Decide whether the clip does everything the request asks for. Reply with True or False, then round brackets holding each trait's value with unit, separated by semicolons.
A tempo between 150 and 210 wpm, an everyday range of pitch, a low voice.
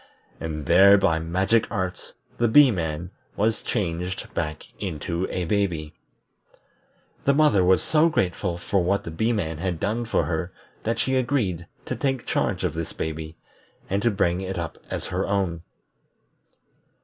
True (160 wpm; 4.2 semitones; 95 Hz)